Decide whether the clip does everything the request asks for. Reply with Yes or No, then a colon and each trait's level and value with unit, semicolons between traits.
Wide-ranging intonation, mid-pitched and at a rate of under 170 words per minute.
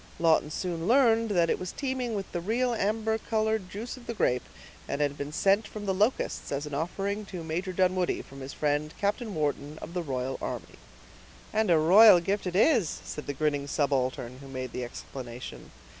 No: wide, 6.7 semitones; medium, 175 Hz; average, 195 wpm